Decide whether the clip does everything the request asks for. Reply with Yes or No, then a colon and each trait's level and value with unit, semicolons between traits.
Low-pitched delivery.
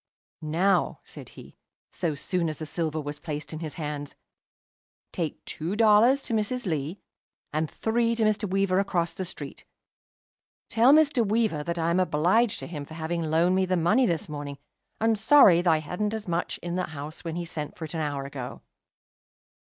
No: medium, 170 Hz